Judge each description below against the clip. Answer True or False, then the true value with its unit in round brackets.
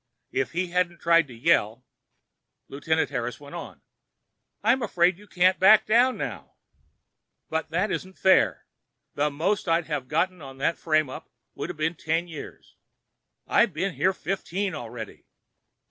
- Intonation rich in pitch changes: False (4.5 semitones)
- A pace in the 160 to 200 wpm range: False (145 wpm)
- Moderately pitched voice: True (165 Hz)